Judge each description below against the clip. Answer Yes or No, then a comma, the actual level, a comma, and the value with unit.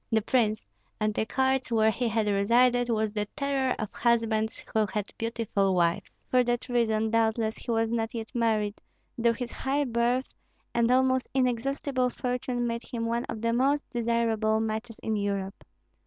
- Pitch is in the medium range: No, high, 230 Hz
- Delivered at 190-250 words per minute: No, average, 170 wpm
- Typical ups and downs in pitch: No, narrow, 2.2 semitones